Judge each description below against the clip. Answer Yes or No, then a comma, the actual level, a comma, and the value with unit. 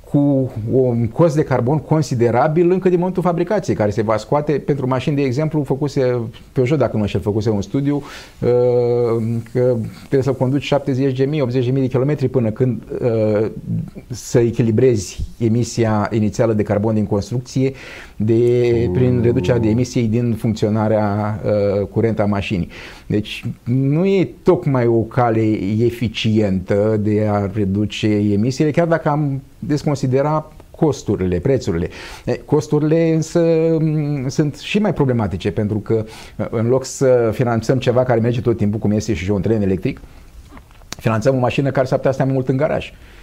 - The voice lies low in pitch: Yes, low, 125 Hz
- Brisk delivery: No, average, 145 wpm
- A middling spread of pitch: Yes, average, 4.4 semitones